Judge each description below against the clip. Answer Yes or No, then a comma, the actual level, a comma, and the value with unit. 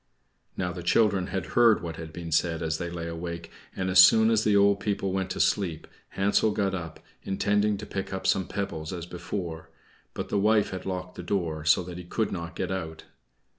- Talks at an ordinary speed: No, fast, 210 wpm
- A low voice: Yes, very low, 90 Hz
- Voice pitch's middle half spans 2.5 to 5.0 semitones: Yes, average, 2.9 semitones